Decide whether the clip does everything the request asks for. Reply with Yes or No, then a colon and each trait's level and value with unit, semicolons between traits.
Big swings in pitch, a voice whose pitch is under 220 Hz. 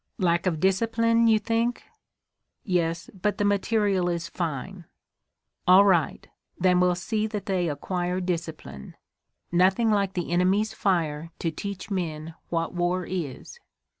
No: average, 3.1 semitones; medium, 185 Hz